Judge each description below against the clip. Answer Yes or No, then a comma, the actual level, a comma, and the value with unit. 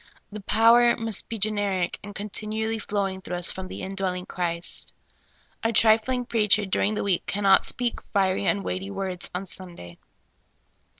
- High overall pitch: Yes, high, 200 Hz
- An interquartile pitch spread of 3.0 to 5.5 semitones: No, narrow, 2.5 semitones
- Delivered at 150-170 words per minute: Yes, average, 155 wpm